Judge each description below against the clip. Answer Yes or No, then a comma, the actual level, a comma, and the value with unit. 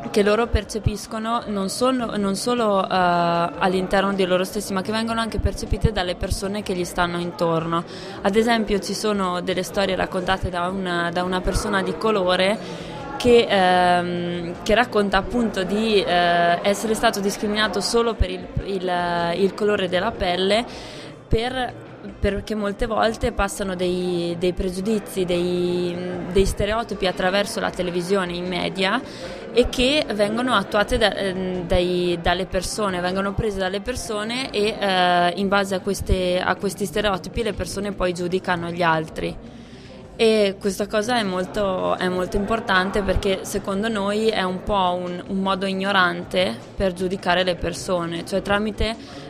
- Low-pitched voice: No, high, 195 Hz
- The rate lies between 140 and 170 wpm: Yes, average, 150 wpm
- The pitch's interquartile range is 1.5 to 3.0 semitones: Yes, narrow, 2.6 semitones